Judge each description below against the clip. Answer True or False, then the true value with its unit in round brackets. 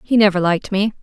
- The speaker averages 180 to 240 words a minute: True (235 wpm)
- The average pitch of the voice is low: False (200 Hz)